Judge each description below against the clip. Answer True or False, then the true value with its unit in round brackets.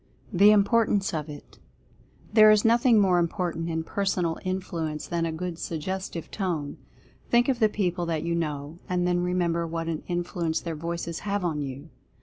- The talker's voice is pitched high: False (175 Hz)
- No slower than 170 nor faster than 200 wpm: True (175 wpm)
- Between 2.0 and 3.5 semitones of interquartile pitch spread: True (2.9 semitones)